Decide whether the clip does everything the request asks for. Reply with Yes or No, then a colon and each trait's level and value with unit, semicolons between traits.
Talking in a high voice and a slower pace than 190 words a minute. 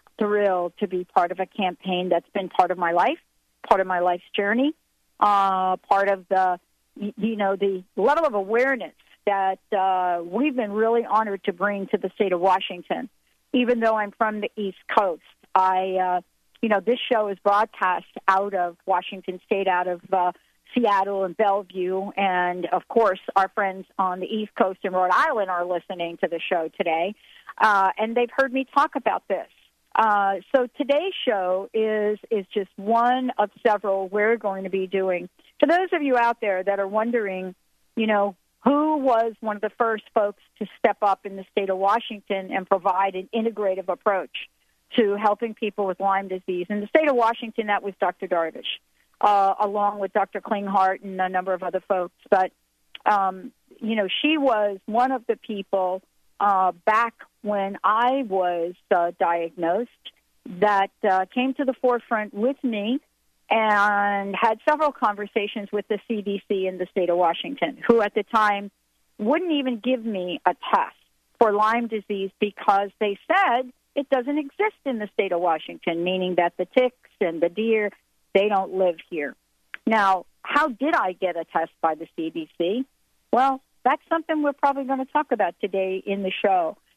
Yes: high, 205 Hz; average, 180 wpm